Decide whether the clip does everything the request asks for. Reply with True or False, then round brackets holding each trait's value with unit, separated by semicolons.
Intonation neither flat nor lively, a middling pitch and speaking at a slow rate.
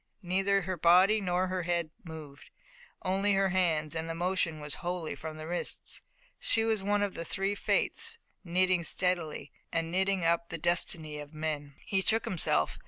False (3.0 semitones; 175 Hz; 170 wpm)